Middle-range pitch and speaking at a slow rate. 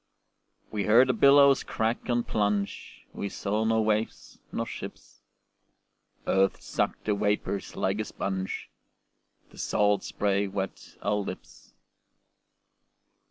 No: low, 105 Hz; slow, 115 wpm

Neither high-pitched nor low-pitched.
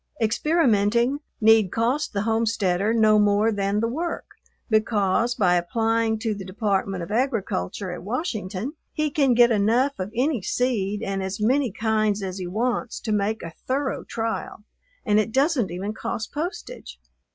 No: high, 220 Hz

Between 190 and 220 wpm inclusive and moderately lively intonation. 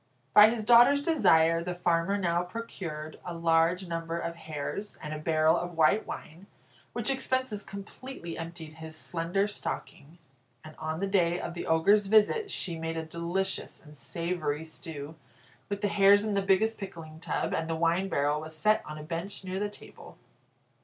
No: average, 175 wpm; average, 3.8 semitones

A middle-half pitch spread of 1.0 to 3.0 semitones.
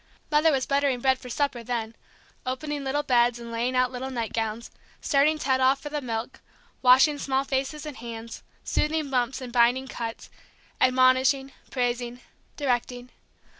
Yes: narrow, 2.4 semitones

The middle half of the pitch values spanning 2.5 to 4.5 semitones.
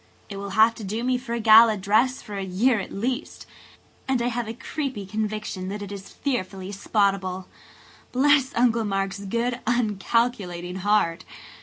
Yes: average, 3.7 semitones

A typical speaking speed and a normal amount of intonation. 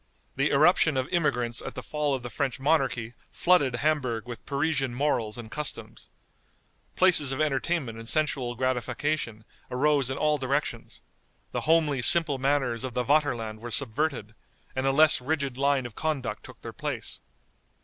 Yes: average, 160 wpm; average, 3.6 semitones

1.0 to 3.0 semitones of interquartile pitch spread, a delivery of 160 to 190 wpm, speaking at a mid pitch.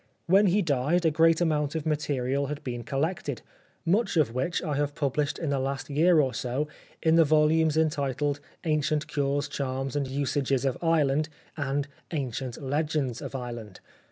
Yes: average, 2.7 semitones; average, 180 wpm; medium, 145 Hz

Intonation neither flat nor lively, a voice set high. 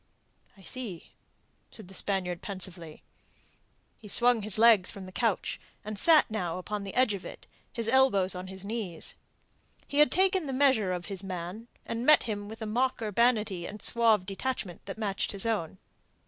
Yes: average, 3.9 semitones; high, 210 Hz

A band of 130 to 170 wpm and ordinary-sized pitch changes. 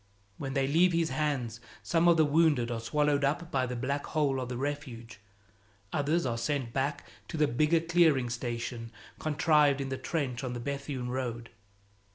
No: average, 180 wpm; average, 3.7 semitones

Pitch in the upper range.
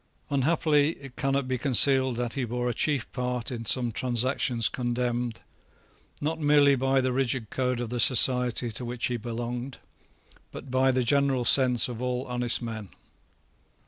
No: low, 125 Hz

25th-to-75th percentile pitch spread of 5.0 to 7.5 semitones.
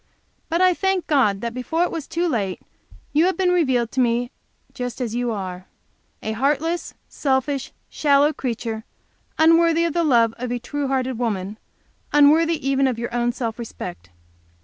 Yes: average, 5.3 semitones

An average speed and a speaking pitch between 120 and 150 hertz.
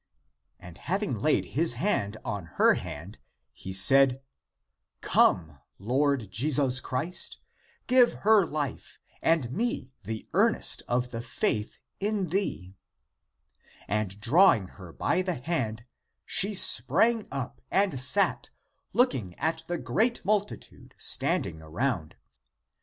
No: slow, 115 wpm; low, 135 Hz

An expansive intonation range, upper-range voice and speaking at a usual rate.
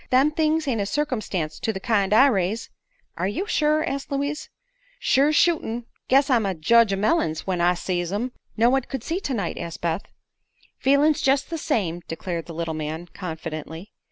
Yes: wide, 8.0 semitones; high, 220 Hz; average, 185 wpm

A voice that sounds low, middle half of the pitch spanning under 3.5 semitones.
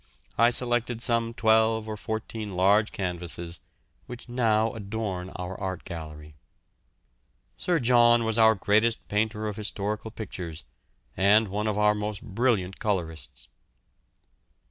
Yes: low, 105 Hz; average, 3.0 semitones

